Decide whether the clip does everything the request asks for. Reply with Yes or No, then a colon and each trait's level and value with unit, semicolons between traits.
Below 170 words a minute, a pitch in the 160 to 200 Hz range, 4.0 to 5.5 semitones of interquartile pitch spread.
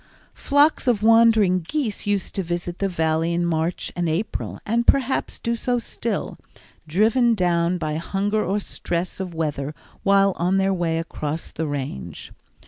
Yes: average, 155 wpm; medium, 185 Hz; average, 4.7 semitones